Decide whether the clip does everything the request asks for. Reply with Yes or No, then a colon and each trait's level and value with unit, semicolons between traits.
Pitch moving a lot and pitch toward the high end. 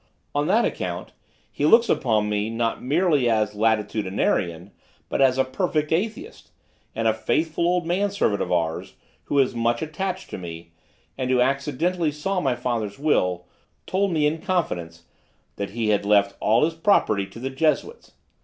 No: wide, 7.5 semitones; low, 130 Hz